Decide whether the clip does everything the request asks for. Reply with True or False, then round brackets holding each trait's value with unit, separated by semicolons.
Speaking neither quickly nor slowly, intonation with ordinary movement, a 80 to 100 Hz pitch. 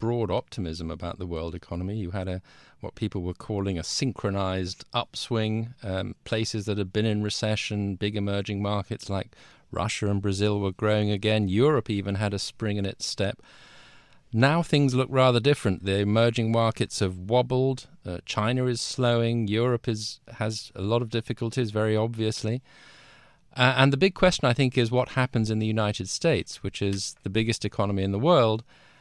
False (180 wpm; 3.1 semitones; 110 Hz)